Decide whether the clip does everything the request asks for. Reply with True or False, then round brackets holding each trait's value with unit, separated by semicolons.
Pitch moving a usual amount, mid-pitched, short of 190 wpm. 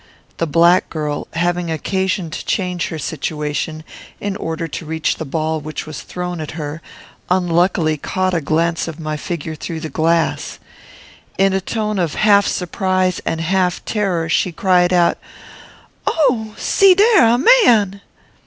True (3.2 semitones; 175 Hz; 155 wpm)